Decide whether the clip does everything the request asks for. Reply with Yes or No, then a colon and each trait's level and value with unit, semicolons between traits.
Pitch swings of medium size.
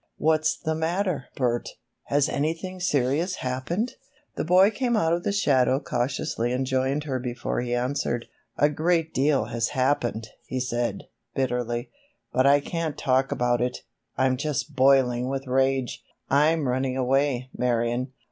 Yes: average, 3.7 semitones